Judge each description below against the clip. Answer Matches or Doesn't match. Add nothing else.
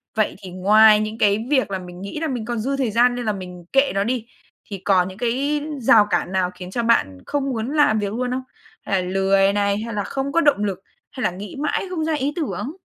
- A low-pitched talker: Doesn't match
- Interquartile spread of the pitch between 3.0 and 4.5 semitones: Doesn't match